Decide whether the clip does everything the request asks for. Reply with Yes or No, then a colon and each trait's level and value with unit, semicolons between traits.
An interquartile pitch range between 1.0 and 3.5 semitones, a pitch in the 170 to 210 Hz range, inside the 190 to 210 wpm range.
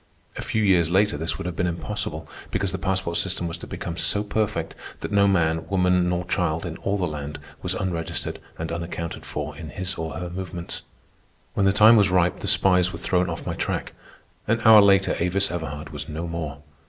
No: average, 2.8 semitones; very low, 90 Hz; fast, 205 wpm